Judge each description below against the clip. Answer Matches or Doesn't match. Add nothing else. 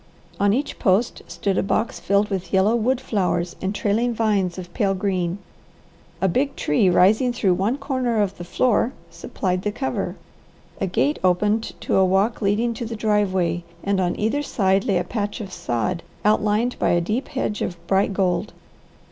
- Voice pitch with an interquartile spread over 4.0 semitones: Doesn't match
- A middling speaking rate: Matches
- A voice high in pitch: Matches